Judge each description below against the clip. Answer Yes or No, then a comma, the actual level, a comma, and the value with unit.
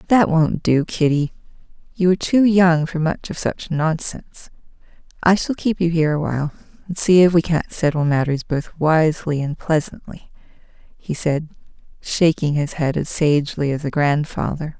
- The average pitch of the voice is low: No, medium, 160 Hz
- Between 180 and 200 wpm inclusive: No, average, 165 wpm